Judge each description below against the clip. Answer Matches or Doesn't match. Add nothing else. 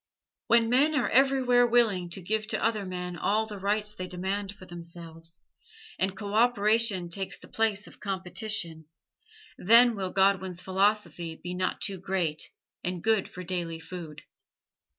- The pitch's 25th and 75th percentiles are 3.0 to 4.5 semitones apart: Matches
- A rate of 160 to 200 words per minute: Doesn't match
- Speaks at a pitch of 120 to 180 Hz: Doesn't match